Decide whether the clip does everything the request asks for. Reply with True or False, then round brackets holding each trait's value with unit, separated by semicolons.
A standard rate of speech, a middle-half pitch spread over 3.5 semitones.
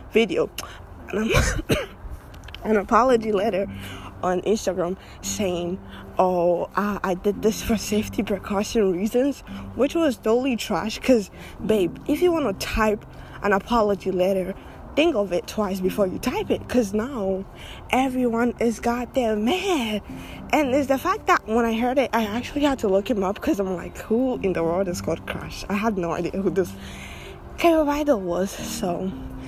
True (165 wpm; 4.6 semitones)